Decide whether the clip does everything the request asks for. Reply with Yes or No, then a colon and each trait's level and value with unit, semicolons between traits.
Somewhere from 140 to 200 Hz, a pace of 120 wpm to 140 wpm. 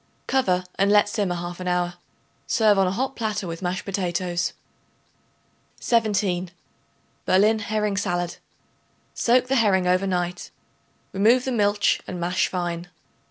Yes: high, 190 Hz; slow, 135 wpm